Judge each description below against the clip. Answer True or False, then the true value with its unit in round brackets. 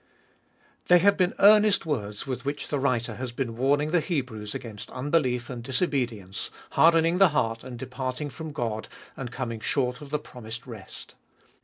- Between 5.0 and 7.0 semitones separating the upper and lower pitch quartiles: False (4.3 semitones)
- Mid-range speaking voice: False (130 Hz)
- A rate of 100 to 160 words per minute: False (170 wpm)